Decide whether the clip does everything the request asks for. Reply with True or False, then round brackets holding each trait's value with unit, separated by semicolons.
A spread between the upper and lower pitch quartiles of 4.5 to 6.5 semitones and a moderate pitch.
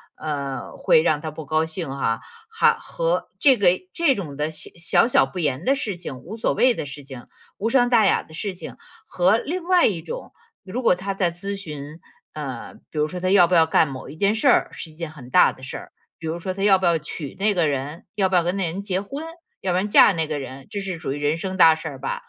True (4.8 semitones; 175 Hz)